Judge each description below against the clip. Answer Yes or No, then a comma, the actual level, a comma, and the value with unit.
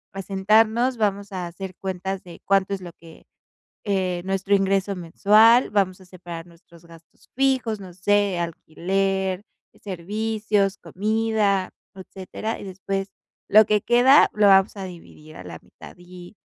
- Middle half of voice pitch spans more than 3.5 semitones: No, narrow, 2.6 semitones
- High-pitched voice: Yes, high, 195 Hz